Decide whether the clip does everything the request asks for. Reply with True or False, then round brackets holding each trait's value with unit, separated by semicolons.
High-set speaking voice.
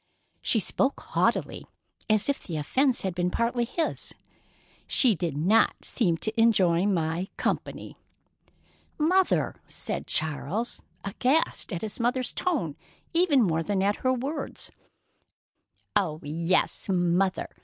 True (205 Hz)